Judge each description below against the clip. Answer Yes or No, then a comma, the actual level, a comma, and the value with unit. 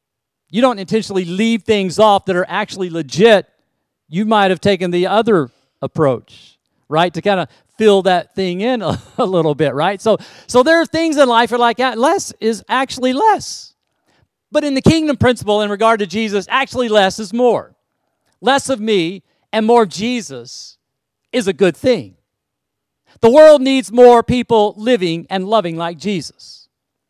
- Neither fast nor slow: Yes, average, 170 wpm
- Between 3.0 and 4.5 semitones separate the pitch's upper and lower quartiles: No, average, 5.0 semitones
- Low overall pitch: No, high, 210 Hz